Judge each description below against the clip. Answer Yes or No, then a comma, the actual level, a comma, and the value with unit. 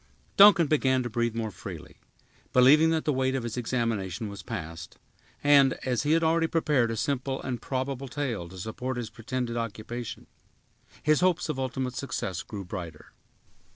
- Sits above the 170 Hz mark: No, low, 125 Hz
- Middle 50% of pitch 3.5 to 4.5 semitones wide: Yes, average, 4.0 semitones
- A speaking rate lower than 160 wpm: No, average, 165 wpm